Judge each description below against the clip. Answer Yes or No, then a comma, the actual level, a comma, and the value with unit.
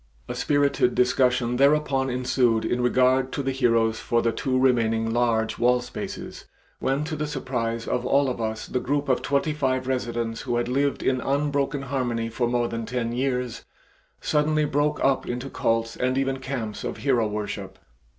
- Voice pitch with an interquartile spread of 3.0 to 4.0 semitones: No, narrow, 2.6 semitones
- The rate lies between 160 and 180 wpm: Yes, average, 175 wpm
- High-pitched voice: No, low, 125 Hz